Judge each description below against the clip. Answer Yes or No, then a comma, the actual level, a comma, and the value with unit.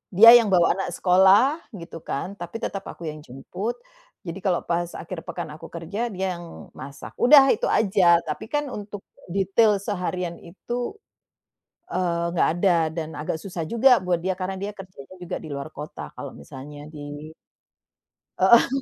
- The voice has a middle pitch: Yes, medium, 180 Hz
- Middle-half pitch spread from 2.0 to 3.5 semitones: Yes, average, 2.9 semitones